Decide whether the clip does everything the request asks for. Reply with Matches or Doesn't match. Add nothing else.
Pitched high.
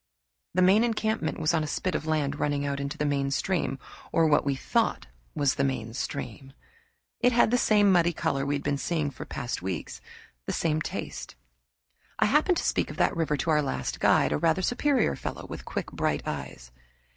Doesn't match